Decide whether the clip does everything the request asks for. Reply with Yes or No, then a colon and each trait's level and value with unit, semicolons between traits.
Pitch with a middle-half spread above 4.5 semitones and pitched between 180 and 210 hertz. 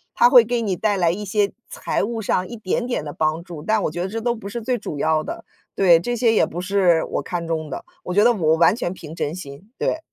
Yes: average, 5.1 semitones; high, 190 Hz